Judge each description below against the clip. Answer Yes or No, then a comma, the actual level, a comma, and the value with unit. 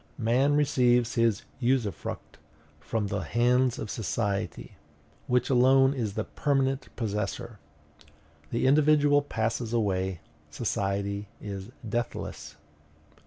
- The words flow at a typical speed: No, slow, 100 wpm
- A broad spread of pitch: No, average, 4.1 semitones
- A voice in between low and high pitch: No, low, 120 Hz